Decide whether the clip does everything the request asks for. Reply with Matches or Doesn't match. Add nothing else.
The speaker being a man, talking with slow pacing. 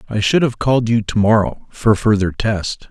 Doesn't match